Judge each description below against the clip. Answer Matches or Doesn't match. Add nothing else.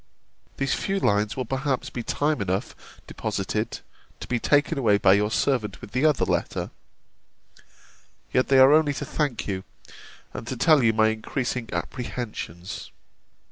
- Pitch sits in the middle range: Doesn't match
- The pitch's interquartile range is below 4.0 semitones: Doesn't match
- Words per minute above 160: Doesn't match